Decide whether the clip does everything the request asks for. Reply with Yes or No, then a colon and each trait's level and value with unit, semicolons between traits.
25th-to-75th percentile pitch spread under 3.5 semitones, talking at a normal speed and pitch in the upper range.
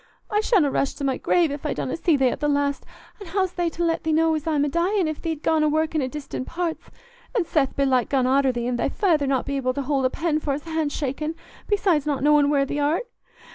No: average, 2.9 semitones; fast, 250 wpm; very high, 300 Hz